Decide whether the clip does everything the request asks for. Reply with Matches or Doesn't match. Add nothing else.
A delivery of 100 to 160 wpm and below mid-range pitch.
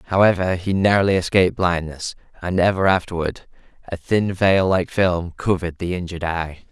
Matches